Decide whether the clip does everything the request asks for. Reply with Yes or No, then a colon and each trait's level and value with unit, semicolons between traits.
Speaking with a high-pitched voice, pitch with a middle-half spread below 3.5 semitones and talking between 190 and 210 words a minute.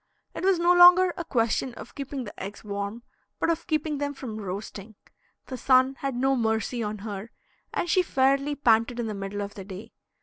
No: high, 245 Hz; average, 5.3 semitones; average, 200 wpm